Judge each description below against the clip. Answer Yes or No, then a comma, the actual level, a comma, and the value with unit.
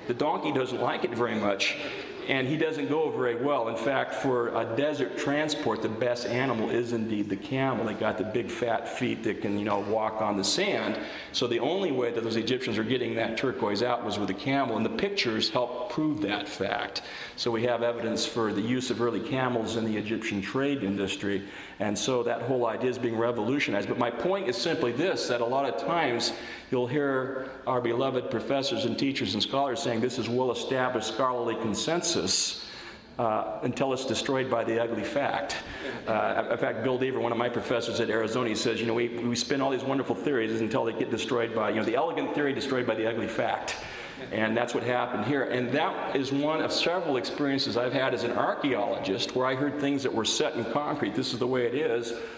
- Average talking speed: No, fast, 220 wpm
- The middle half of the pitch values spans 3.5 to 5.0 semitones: No, average, 2.8 semitones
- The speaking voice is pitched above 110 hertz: Yes, low, 120 Hz